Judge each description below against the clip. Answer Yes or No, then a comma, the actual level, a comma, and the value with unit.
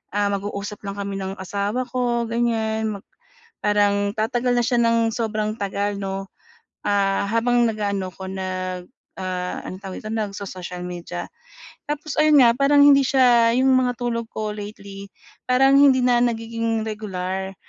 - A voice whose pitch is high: Yes, high, 215 Hz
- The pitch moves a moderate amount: Yes, average, 3.4 semitones